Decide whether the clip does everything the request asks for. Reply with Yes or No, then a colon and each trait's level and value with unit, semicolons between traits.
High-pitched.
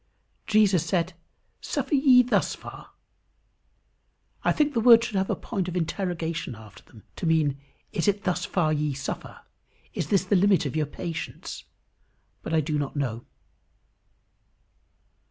No: medium, 175 Hz